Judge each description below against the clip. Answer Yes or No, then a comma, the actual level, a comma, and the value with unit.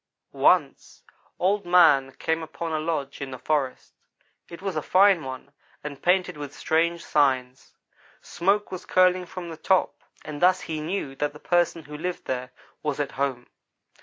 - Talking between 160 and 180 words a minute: Yes, average, 165 wpm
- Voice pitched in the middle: Yes, medium, 160 Hz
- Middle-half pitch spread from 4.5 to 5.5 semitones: No, average, 4.1 semitones